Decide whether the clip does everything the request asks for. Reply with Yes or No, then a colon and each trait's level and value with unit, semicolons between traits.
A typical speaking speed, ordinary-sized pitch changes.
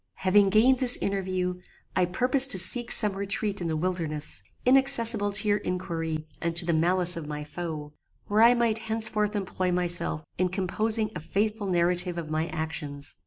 Yes: average, 170 wpm; average, 4.1 semitones